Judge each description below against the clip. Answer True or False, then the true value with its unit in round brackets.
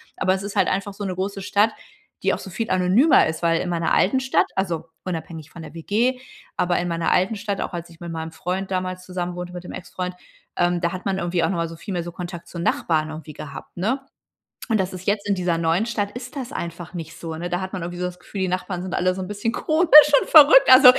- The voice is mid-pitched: True (180 Hz)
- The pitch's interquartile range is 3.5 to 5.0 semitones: False (2.8 semitones)